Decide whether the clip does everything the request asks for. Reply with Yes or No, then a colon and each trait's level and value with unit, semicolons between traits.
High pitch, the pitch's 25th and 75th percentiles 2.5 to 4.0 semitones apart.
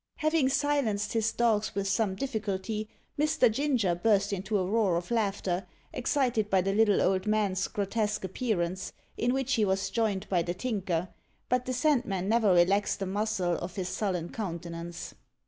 Yes: high, 205 Hz; average, 3.5 semitones